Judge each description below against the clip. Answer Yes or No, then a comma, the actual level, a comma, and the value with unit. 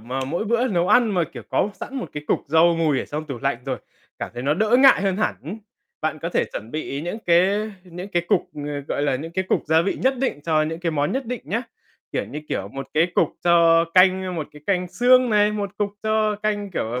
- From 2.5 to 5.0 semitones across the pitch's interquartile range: No, wide, 5.6 semitones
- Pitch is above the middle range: No, medium, 175 Hz